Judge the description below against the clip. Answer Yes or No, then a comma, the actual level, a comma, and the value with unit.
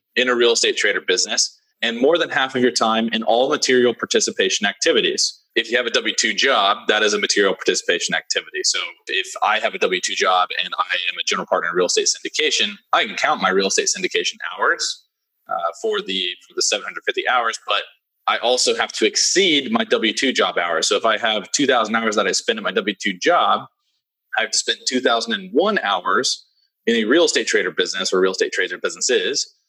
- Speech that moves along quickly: Yes, fast, 220 wpm